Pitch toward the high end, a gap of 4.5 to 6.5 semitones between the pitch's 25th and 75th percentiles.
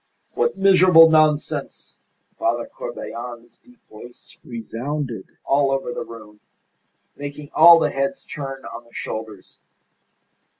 No: low, 135 Hz; wide, 5.5 semitones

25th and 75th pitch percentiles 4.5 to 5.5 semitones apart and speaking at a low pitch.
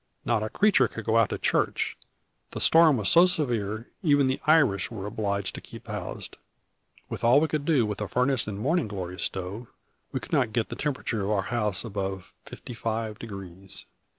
Yes: average, 5.0 semitones; low, 110 Hz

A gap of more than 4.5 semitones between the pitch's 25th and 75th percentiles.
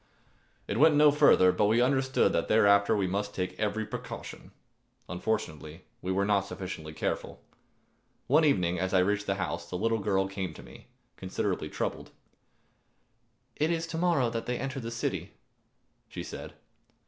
Yes: average, 4.9 semitones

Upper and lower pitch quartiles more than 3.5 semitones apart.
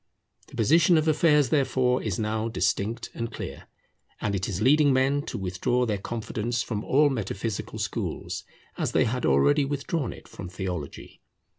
Yes: average, 5.2 semitones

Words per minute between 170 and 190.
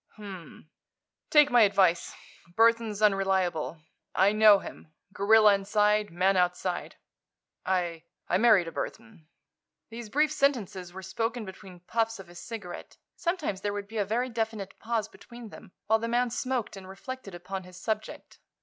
No: average, 155 wpm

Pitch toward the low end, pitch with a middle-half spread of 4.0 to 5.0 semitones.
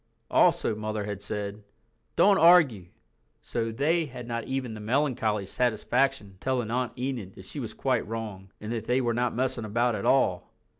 No: low, 115 Hz; average, 3.5 semitones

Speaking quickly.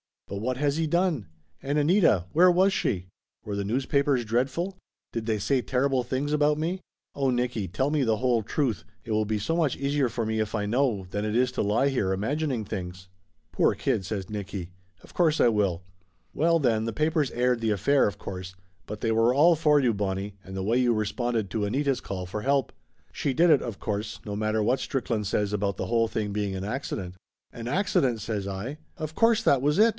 Yes: fast, 220 wpm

